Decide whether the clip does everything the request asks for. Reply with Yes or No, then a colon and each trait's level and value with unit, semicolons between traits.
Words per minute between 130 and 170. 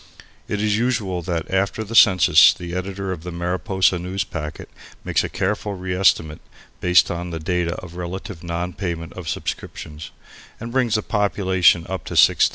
Yes: average, 165 wpm